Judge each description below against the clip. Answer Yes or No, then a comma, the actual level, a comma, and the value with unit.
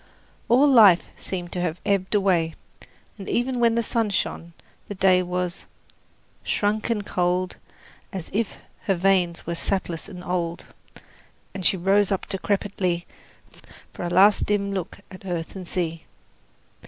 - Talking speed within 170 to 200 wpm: No, average, 145 wpm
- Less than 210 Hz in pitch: Yes, high, 190 Hz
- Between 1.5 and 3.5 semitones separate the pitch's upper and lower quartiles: Yes, narrow, 2.5 semitones